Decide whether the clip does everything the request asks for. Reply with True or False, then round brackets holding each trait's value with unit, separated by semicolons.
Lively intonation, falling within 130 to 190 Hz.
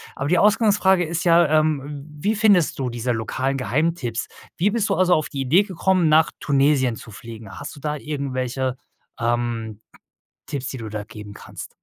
True (6.0 semitones; 140 Hz)